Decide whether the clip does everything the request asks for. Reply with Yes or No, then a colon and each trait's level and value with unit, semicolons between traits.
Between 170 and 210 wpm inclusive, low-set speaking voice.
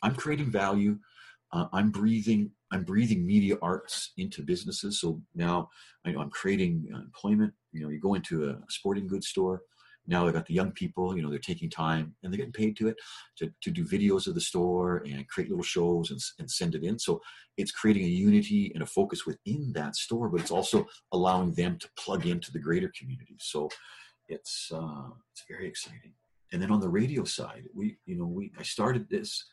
Yes: fast, 205 wpm; low, 110 Hz